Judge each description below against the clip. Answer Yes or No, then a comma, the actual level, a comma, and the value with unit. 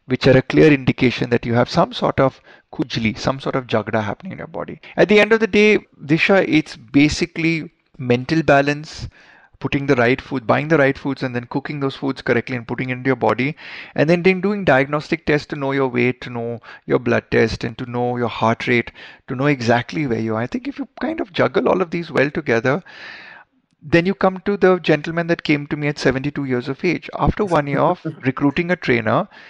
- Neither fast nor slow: No, fast, 230 wpm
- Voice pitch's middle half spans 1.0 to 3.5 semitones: No, average, 5.1 semitones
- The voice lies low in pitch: No, medium, 145 Hz